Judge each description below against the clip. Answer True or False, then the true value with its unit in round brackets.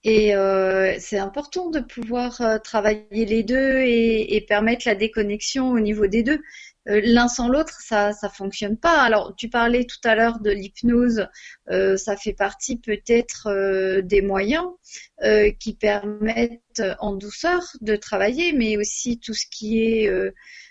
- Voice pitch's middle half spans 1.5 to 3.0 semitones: True (2.7 semitones)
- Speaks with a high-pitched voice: True (220 Hz)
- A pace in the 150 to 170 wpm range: True (160 wpm)